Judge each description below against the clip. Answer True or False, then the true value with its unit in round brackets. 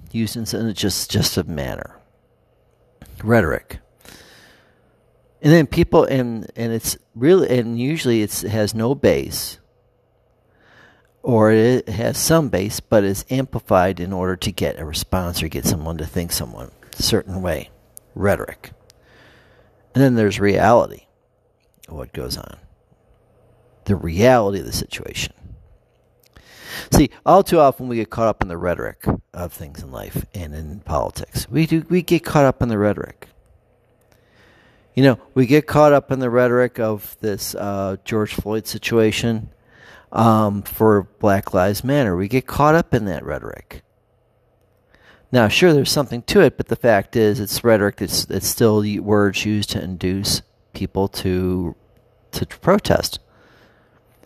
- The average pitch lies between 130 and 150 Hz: False (110 Hz)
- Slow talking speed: False (150 wpm)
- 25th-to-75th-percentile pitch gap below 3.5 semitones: False (4.2 semitones)